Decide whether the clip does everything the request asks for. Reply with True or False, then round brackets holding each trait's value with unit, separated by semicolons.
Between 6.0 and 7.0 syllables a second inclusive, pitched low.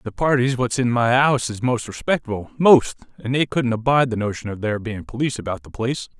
True (6.2 syllables/s; 120 Hz)